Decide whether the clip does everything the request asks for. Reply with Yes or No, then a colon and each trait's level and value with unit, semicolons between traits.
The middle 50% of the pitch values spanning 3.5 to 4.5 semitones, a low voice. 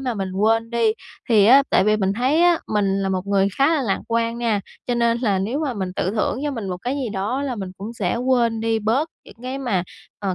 No: average, 4.0 semitones; high, 225 Hz